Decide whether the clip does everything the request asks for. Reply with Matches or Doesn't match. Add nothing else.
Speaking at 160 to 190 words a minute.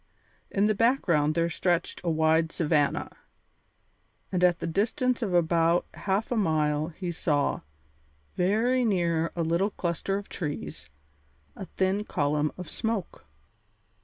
Doesn't match